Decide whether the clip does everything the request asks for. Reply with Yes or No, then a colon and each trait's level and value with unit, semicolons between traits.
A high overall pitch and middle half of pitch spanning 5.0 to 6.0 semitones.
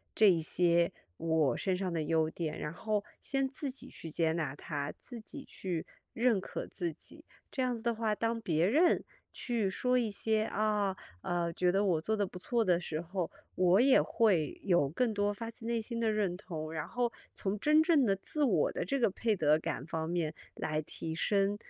Yes: high, 195 Hz; wide, 5.6 semitones